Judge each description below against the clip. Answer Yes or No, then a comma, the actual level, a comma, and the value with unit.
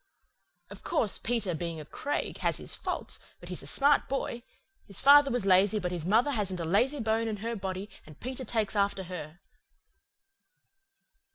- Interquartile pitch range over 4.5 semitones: Yes, average, 4.9 semitones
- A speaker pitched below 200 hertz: No, high, 210 Hz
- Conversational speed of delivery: Yes, average, 175 wpm